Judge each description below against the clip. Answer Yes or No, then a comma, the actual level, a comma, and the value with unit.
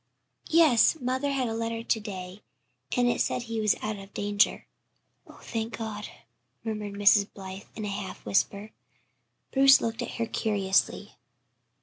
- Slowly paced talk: No, average, 150 wpm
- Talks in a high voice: Yes, high, 220 Hz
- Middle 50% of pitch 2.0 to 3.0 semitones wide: Yes, narrow, 2.5 semitones